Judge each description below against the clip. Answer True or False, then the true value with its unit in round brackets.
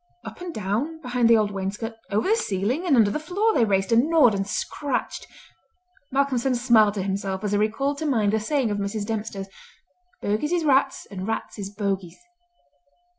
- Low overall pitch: False (225 Hz)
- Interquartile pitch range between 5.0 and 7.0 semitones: True (5.5 semitones)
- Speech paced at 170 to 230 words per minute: True (185 wpm)